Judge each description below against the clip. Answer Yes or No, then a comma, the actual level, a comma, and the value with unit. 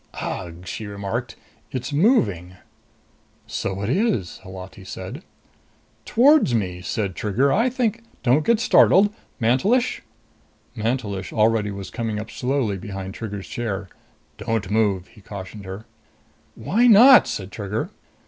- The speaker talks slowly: Yes, slow, 130 wpm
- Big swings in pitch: Yes, wide, 6.3 semitones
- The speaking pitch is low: Yes, low, 110 Hz